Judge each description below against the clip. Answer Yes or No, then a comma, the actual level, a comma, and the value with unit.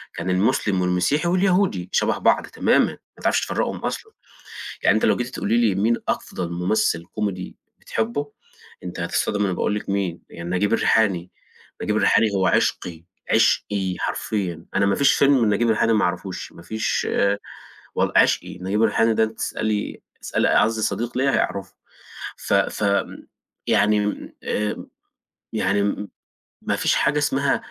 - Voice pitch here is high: No, low, 105 Hz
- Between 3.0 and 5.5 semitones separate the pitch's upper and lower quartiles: Yes, average, 3.4 semitones